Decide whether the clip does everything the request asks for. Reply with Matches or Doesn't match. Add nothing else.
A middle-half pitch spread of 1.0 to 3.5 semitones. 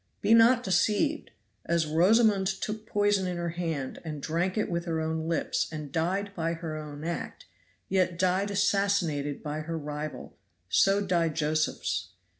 Doesn't match